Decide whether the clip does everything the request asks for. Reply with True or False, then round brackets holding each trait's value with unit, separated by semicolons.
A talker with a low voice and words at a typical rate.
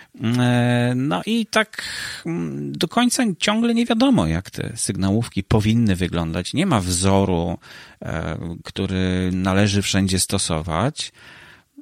False (110 Hz; 100 wpm)